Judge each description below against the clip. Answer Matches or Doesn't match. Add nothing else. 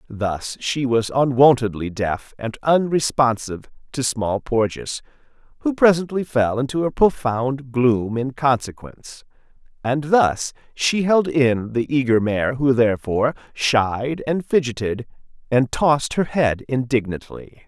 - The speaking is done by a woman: Doesn't match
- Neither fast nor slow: Doesn't match